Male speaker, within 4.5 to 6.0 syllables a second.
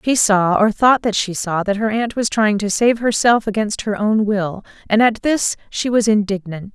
No: female; 4.6 syllables/s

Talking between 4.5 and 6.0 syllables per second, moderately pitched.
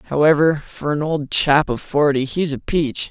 No: 4.2 syllables/s; medium, 150 Hz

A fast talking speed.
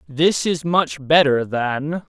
No: average, 140 wpm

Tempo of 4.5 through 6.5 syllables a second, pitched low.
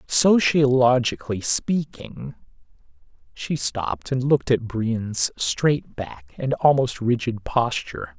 No: 3.7 syllables/s; low, 120 Hz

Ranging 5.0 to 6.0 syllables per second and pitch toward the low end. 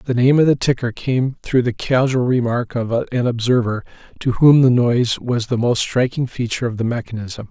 Yes: 5.1 syllables/s; low, 125 Hz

